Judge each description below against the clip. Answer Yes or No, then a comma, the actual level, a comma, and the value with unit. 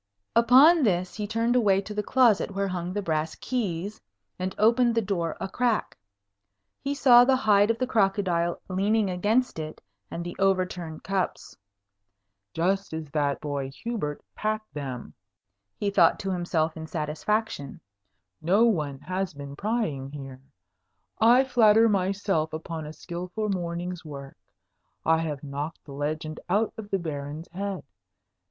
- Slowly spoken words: No, average, 145 wpm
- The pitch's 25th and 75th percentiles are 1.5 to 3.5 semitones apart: No, wide, 5.4 semitones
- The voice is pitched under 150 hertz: No, medium, 185 Hz